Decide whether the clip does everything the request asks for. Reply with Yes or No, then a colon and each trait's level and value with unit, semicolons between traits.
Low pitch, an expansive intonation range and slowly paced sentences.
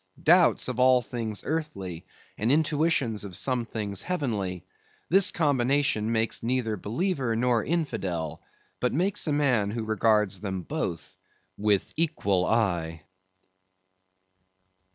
Yes: low, 115 Hz; wide, 6.4 semitones; slow, 115 wpm